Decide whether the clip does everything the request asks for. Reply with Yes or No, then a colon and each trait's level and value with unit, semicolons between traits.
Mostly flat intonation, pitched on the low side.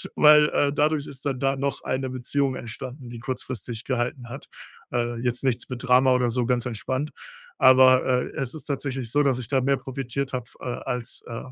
Yes: narrow, 1.9 semitones; low, 130 Hz